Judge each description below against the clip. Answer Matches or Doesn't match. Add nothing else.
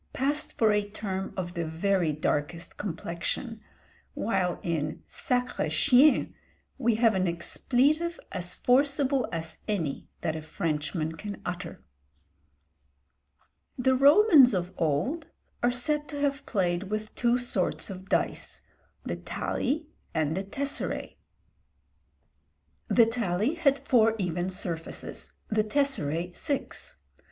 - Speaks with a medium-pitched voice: Doesn't match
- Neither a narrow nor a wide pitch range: Doesn't match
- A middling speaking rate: Doesn't match